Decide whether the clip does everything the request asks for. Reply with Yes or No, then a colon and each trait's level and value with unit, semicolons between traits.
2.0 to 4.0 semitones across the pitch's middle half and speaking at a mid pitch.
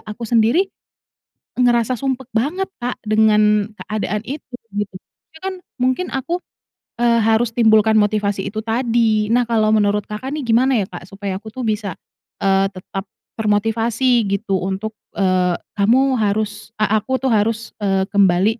No: average, 2.8 semitones; high, 220 Hz